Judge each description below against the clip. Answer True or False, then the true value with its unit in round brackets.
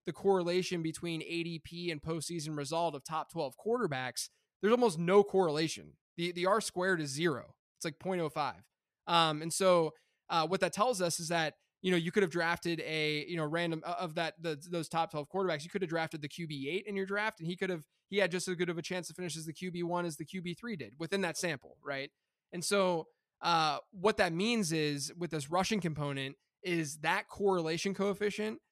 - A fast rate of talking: True (215 wpm)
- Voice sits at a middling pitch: True (170 Hz)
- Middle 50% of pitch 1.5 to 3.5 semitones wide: True (2.7 semitones)